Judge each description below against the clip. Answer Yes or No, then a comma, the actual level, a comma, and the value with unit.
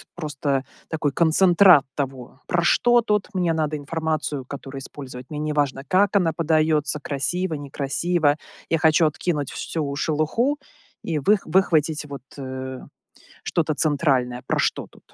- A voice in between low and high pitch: Yes, medium, 155 Hz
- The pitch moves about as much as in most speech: Yes, average, 3.2 semitones